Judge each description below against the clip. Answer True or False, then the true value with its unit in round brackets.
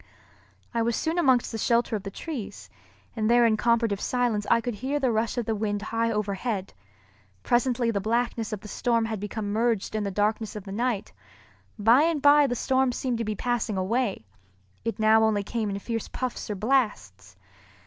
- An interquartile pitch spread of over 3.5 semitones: False (2.6 semitones)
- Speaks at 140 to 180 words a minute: False (195 wpm)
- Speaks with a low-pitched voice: False (225 Hz)